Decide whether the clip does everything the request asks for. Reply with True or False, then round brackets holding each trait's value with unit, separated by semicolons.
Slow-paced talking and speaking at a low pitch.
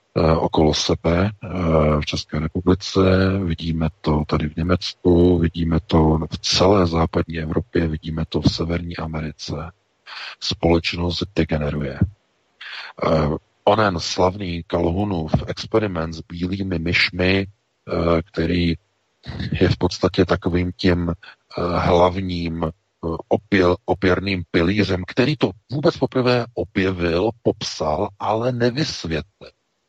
True (95 wpm; 90 Hz)